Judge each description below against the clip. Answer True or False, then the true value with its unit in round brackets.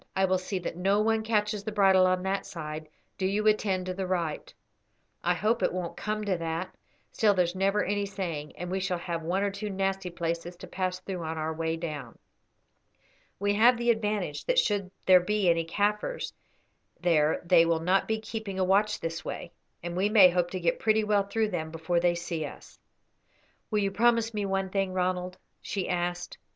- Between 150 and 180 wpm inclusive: False (200 wpm)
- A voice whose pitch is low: False (185 Hz)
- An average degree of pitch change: True (3.0 semitones)